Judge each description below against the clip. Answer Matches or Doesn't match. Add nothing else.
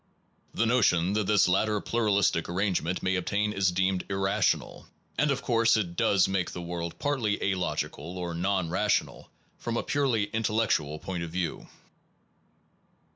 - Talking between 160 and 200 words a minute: Doesn't match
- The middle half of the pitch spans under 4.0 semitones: Matches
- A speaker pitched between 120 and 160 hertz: Doesn't match